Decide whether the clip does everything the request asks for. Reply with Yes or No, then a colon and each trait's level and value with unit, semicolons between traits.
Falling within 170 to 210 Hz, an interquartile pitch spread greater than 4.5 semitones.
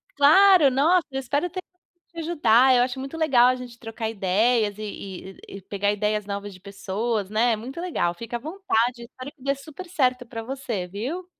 No: high, 245 Hz; average, 5.0 semitones